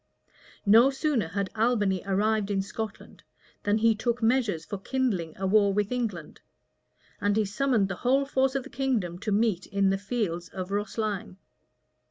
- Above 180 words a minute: No, average, 165 wpm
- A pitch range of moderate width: Yes, average, 3.5 semitones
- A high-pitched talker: Yes, high, 210 Hz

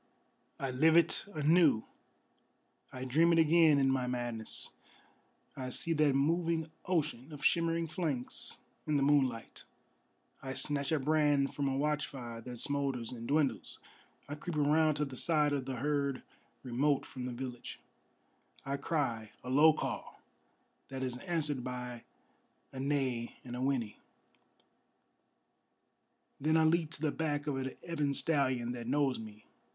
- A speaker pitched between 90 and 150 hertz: Yes, medium, 140 Hz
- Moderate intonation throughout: Yes, average, 3.3 semitones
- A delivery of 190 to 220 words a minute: No, average, 145 wpm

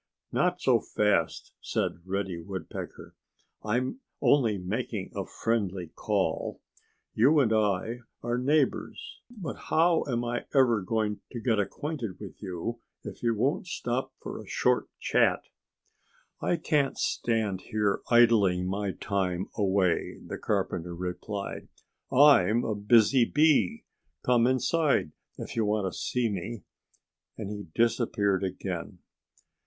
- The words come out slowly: Yes, slow, 125 wpm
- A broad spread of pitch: No, average, 4.3 semitones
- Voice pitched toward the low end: Yes, low, 110 Hz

